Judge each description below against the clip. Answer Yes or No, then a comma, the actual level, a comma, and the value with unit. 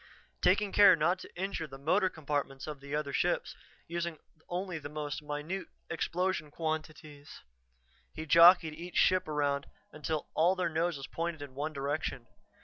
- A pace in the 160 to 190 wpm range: No, average, 150 wpm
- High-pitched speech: No, medium, 155 Hz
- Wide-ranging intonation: No, average, 3.0 semitones